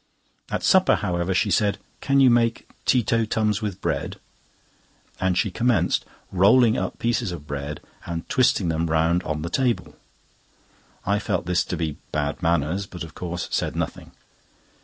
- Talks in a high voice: No, very low, 95 Hz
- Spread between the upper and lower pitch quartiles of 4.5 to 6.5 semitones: Yes, average, 5.2 semitones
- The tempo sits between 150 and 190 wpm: Yes, average, 160 wpm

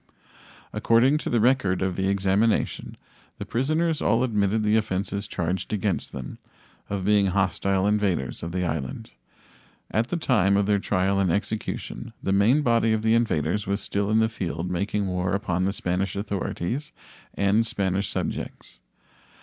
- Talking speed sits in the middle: Yes, average, 155 wpm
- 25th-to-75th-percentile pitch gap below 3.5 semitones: Yes, average, 2.9 semitones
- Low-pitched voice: Yes, low, 100 Hz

